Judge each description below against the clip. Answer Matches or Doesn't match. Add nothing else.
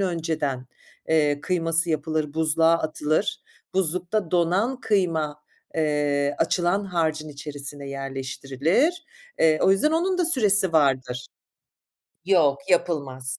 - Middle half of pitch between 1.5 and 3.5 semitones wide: Doesn't match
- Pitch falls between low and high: Matches